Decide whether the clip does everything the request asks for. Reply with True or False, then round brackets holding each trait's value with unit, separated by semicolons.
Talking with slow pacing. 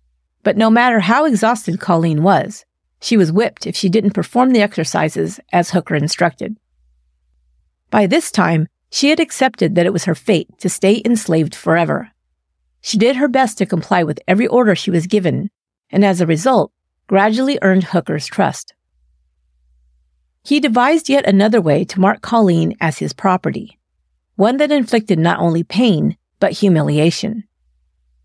False (155 wpm)